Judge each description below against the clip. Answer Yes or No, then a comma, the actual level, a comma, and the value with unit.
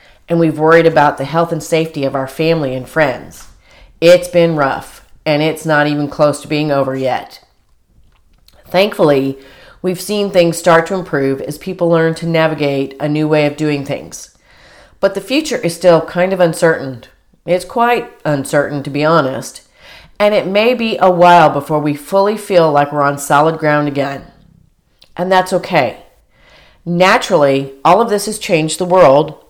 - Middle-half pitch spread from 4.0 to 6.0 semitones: No, average, 3.6 semitones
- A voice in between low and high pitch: Yes, medium, 160 Hz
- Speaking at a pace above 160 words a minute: Yes, average, 170 wpm